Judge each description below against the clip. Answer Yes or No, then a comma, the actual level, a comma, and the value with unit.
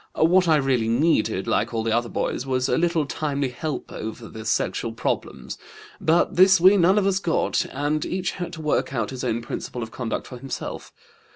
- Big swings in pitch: Yes, wide, 6.1 semitones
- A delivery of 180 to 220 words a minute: Yes, average, 200 wpm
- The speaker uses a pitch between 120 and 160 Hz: Yes, low, 135 Hz